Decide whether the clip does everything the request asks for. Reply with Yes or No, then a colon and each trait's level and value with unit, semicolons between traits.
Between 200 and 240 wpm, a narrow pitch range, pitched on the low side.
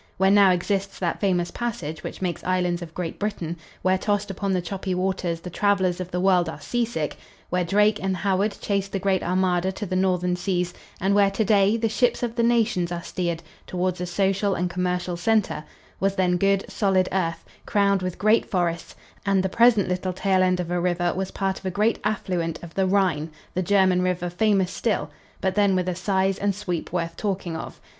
No: fast, 205 wpm; narrow, 1.9 semitones; medium, 185 Hz